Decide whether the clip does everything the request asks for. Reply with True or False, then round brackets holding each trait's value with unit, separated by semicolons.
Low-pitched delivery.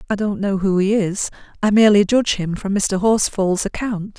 False (200 Hz)